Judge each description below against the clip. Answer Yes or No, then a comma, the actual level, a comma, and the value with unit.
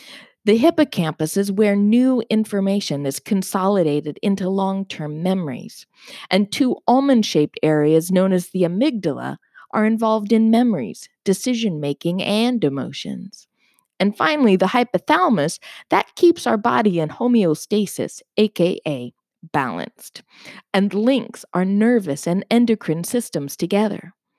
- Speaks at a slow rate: Yes, slow, 120 wpm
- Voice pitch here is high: Yes, high, 200 Hz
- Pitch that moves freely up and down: No, average, 4.8 semitones